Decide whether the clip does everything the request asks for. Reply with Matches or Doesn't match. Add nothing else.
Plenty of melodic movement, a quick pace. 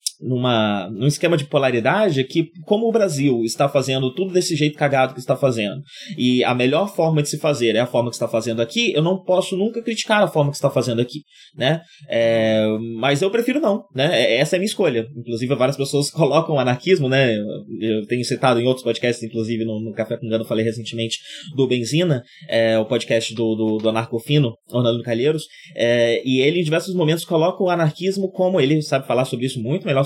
Matches